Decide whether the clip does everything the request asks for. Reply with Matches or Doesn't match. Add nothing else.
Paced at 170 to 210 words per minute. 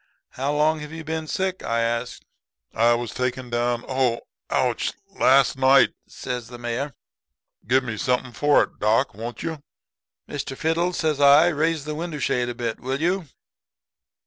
Doesn't match